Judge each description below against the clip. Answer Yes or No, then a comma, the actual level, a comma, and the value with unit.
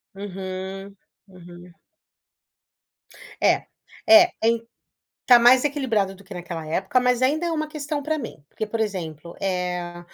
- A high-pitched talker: Yes, high, 200 Hz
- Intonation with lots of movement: Yes, wide, 6.3 semitones